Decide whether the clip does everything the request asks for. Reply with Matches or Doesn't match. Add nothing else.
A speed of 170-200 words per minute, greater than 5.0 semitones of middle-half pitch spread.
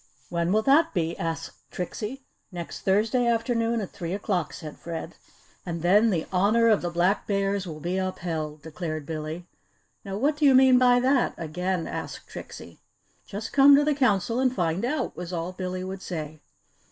Matches